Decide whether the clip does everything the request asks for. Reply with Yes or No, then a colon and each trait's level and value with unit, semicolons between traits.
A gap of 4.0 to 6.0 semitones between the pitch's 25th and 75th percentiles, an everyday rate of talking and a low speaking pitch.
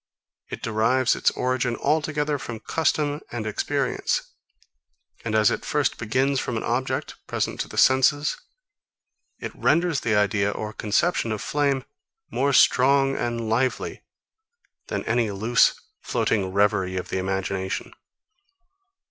No: average, 4.4 semitones; slow, 130 wpm; low, 120 Hz